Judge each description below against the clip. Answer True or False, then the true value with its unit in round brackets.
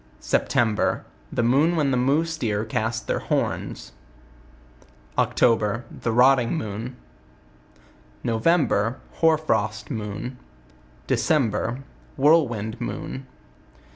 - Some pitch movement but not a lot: True (4.3 semitones)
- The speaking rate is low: True (75 wpm)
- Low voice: True (120 Hz)